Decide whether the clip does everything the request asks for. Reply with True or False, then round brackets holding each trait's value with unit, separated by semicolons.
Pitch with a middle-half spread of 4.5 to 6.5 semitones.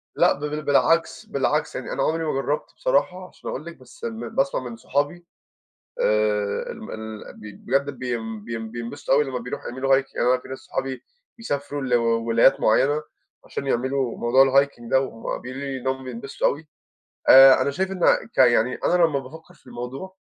False (3.2 semitones)